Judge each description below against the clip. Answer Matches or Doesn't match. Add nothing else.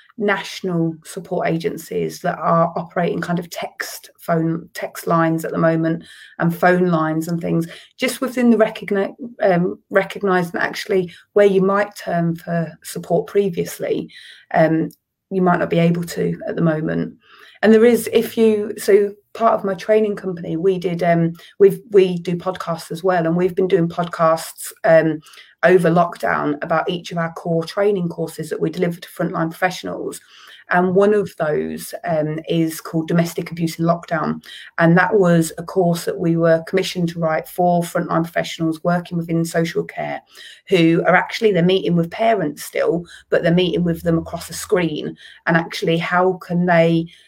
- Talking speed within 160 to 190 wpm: Matches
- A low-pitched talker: Doesn't match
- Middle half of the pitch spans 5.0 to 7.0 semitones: Doesn't match